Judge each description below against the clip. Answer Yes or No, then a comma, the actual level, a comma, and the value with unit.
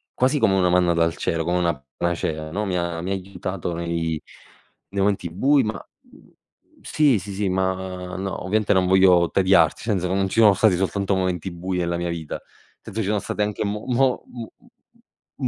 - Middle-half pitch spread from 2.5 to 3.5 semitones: Yes, average, 2.9 semitones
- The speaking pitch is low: Yes, very low, 95 Hz